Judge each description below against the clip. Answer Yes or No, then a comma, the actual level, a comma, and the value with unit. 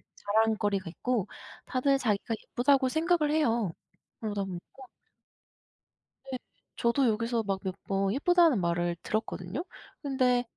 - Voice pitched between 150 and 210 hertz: No, high, 230 Hz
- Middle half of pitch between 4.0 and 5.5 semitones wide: Yes, average, 5.2 semitones